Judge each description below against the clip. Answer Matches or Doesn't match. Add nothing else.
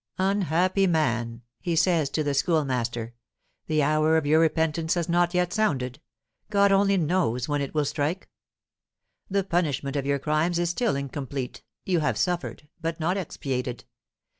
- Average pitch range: Matches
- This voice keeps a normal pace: Matches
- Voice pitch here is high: Doesn't match